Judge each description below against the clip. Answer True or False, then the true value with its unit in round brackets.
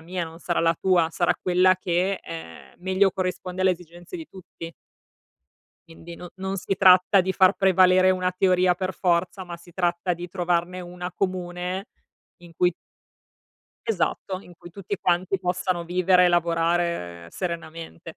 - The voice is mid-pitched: True (180 Hz)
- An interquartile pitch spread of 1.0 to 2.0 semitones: True (1.4 semitones)